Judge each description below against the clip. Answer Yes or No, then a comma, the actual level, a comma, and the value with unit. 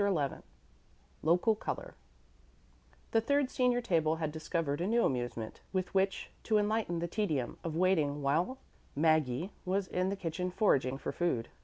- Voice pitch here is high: No, medium, 175 Hz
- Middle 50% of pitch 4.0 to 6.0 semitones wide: Yes, average, 5.1 semitones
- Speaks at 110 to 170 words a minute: Yes, average, 150 wpm